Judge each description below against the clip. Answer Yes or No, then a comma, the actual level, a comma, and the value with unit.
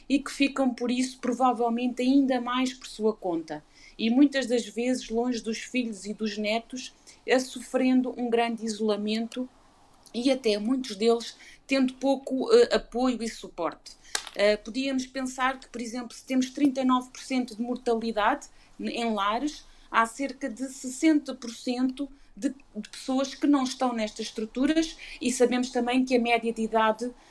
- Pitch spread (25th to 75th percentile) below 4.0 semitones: Yes, narrow, 2.5 semitones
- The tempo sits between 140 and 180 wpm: Yes, average, 150 wpm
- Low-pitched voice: No, very high, 250 Hz